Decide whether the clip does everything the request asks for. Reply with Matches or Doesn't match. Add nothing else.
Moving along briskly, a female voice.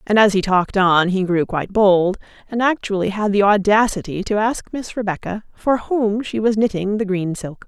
Matches